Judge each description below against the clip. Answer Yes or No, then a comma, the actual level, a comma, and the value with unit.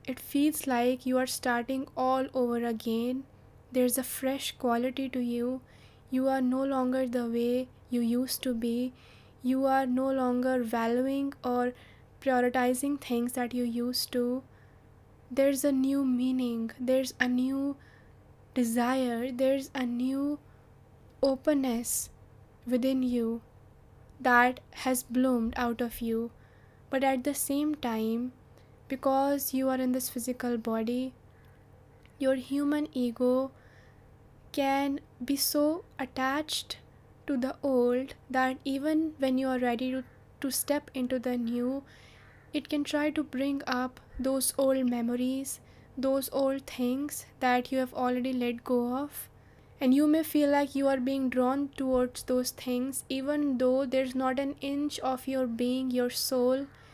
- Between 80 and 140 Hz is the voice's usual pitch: No, very high, 260 Hz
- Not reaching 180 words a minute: Yes, average, 140 wpm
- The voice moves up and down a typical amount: No, narrow, 1.6 semitones